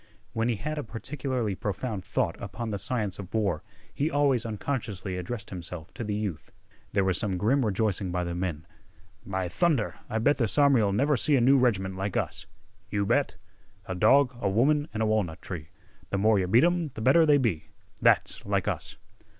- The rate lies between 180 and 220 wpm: Yes, average, 195 wpm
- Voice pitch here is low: Yes, low, 110 Hz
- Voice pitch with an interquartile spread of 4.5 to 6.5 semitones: Yes, average, 5.1 semitones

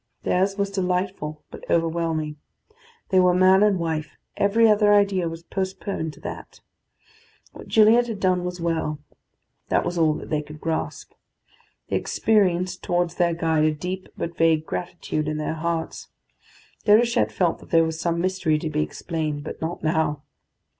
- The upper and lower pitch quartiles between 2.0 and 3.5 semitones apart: Yes, average, 2.9 semitones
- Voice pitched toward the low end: No, medium, 170 Hz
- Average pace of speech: Yes, average, 160 wpm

